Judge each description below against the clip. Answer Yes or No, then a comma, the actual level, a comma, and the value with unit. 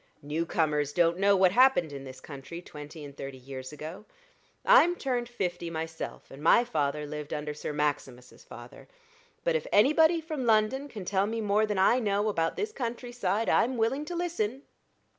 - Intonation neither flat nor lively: No, wide, 8.3 semitones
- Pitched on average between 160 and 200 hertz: Yes, high, 190 Hz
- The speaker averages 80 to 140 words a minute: No, average, 180 wpm